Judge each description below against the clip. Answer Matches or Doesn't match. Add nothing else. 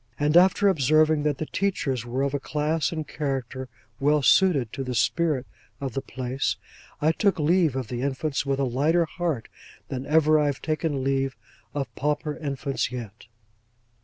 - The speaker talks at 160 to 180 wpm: Matches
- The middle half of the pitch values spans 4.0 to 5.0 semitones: Doesn't match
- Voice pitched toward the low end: Doesn't match